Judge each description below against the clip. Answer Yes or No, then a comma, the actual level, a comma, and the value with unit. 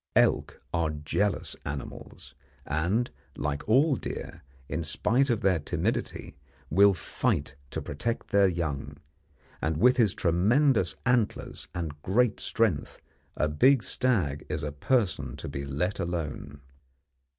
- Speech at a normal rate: No, slow, 130 wpm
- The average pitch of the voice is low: Yes, very low, 90 Hz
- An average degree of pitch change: No, wide, 7.4 semitones